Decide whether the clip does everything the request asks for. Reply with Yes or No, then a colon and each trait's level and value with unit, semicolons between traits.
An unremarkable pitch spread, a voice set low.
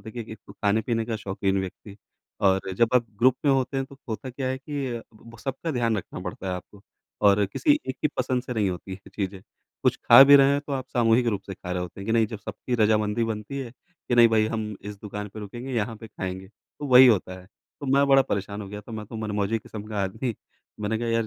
Yes: average, 3.6 semitones; low, 110 Hz